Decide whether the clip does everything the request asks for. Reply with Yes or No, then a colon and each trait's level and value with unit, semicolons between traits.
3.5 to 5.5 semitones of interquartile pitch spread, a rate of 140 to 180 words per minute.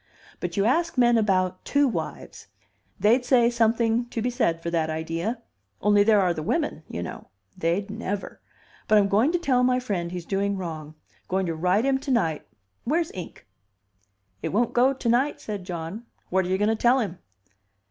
No: average, 5.2 semitones; average, 190 wpm